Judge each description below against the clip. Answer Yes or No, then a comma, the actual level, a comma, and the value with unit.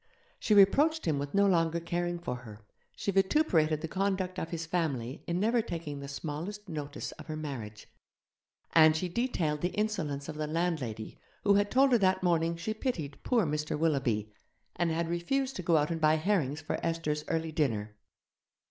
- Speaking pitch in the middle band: Yes, medium, 165 Hz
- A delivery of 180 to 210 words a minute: Yes, average, 185 wpm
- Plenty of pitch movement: No, average, 4.2 semitones